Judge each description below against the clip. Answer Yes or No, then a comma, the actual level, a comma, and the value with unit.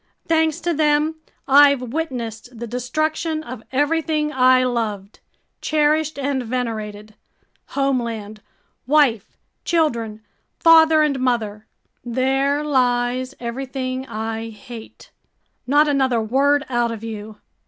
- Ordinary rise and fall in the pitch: Yes, average, 4.3 semitones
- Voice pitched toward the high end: Yes, very high, 255 Hz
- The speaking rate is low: Yes, slow, 100 wpm